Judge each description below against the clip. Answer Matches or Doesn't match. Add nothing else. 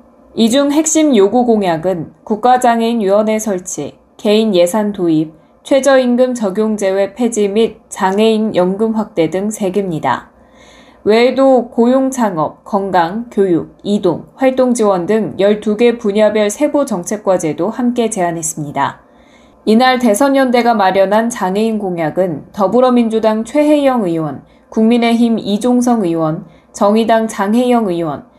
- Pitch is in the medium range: Doesn't match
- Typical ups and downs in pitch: Matches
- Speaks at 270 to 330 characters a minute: Matches